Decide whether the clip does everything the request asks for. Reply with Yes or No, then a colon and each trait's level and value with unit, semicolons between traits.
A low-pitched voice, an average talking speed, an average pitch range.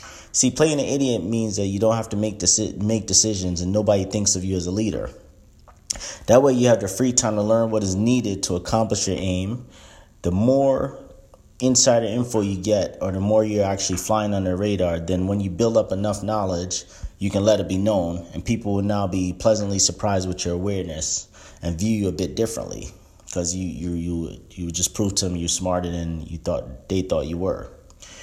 No: low, 100 Hz; fast, 210 wpm; average, 3.1 semitones